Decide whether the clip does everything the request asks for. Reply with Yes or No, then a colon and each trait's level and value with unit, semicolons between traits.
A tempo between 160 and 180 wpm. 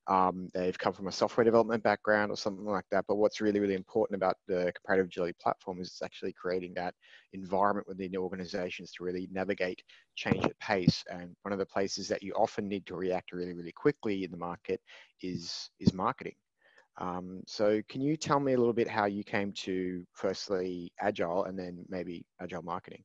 No: average, 200 wpm